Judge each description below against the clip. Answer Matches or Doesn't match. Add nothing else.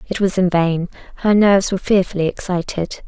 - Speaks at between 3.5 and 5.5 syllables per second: Doesn't match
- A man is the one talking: Doesn't match